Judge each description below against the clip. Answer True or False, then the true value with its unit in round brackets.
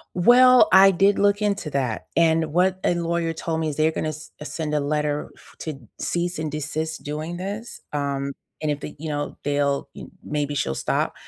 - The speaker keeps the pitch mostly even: False (3.2 semitones)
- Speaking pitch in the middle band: True (155 Hz)